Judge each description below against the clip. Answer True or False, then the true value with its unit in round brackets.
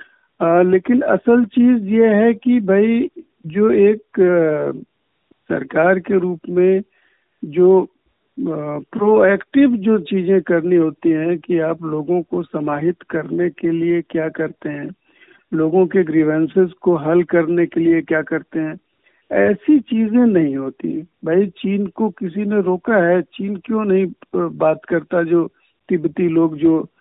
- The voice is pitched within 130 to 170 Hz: False (180 Hz)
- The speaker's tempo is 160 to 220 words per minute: False (140 wpm)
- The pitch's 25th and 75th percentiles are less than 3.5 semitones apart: False (3.8 semitones)